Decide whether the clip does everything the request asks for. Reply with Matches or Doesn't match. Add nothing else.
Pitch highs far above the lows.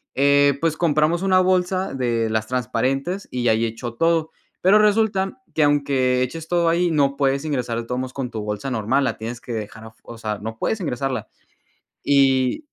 Matches